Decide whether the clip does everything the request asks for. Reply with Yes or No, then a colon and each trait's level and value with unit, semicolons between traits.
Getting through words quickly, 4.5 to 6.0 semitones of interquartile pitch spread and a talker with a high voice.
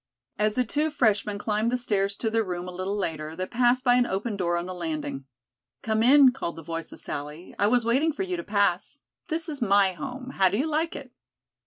Yes: fast, 230 wpm; wide, 5.6 semitones; high, 215 Hz